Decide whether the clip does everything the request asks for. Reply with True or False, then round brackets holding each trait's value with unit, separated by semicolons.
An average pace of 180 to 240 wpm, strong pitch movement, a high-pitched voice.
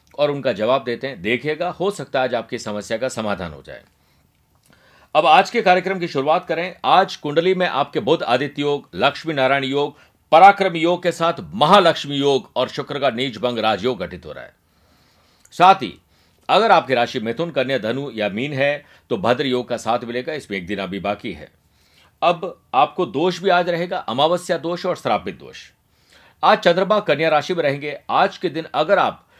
False (190 wpm; 6.0 semitones; 145 Hz)